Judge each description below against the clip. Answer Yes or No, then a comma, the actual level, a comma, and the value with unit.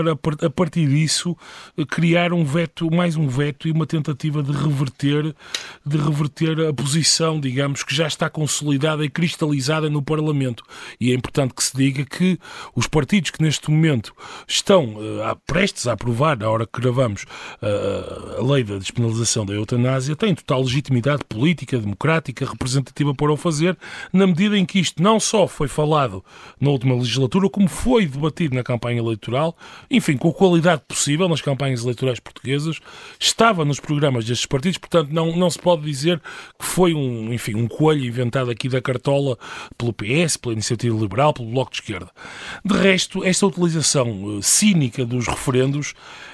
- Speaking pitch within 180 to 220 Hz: No, medium, 150 Hz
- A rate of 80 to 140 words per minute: No, average, 165 wpm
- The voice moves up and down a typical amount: Yes, average, 4.4 semitones